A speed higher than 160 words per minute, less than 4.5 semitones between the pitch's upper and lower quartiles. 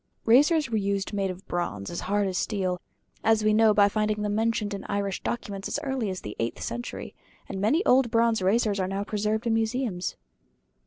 Yes: average, 200 wpm; average, 2.7 semitones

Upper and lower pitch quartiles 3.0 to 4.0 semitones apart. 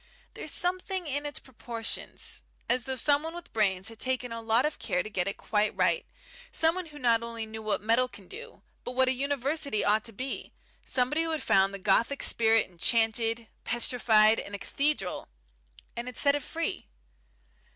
No: average, 4.6 semitones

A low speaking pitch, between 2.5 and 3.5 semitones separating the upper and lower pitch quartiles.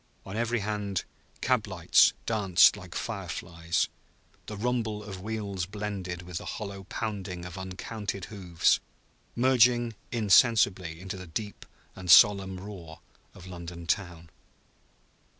Yes: very low, 95 Hz; average, 3.0 semitones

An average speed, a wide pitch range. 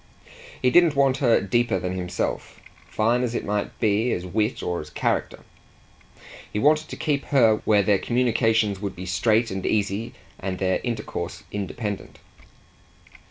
No: average, 155 wpm; average, 4.0 semitones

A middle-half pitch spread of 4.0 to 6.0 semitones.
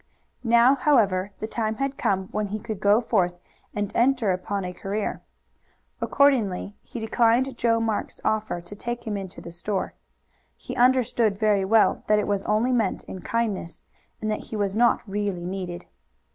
No: average, 3.1 semitones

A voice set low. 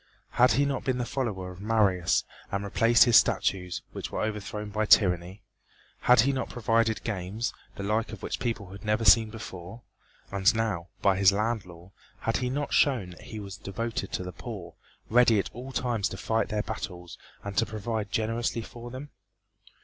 Yes: low, 110 Hz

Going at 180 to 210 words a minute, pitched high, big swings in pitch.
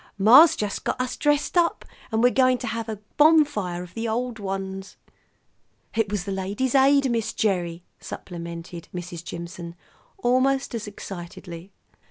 No: average, 150 wpm; high, 210 Hz; wide, 6.1 semitones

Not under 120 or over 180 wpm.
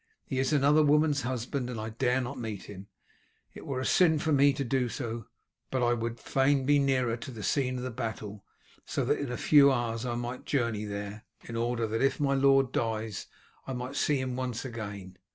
No: fast, 205 wpm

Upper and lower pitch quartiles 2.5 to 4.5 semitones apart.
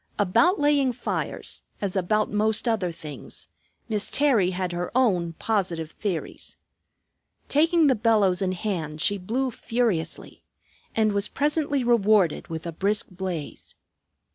No: average, 5.1 semitones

